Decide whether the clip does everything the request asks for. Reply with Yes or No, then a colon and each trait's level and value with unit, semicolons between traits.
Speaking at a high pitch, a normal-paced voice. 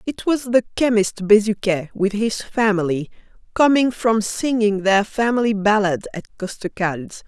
No: high, 215 Hz; slow, 130 wpm